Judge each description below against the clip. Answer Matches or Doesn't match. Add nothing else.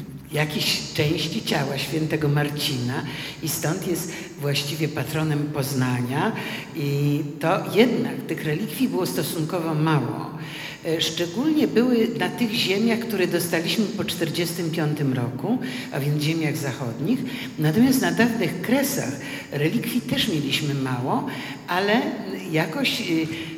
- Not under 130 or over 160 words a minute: Doesn't match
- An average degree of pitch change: Matches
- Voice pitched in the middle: Matches